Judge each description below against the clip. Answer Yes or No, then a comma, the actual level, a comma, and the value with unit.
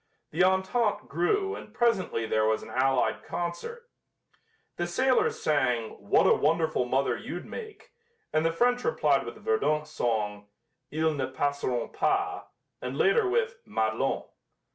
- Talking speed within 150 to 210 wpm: No, average, 140 wpm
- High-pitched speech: No, medium, 170 Hz